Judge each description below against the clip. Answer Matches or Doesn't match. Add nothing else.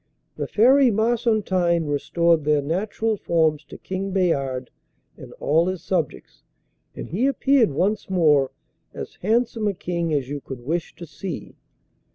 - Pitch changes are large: Matches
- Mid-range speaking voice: Matches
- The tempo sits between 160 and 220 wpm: Doesn't match